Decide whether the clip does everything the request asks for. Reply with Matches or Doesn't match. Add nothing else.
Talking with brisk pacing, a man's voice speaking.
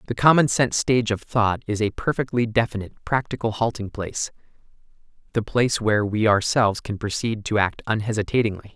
Doesn't match